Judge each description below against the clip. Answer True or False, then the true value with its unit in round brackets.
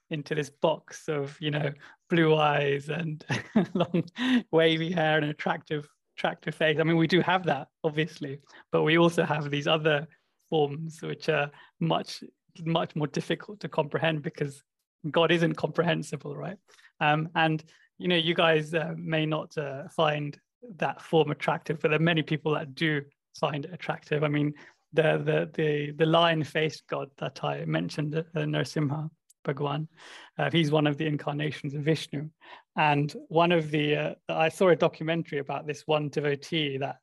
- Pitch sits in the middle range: True (155 Hz)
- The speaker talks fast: False (170 wpm)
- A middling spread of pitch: False (1.7 semitones)